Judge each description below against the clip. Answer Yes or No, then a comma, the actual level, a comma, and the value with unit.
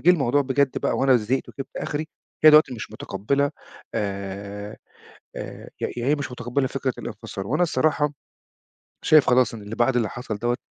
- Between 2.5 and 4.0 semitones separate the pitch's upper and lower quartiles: No, average, 4.6 semitones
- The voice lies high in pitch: No, low, 125 Hz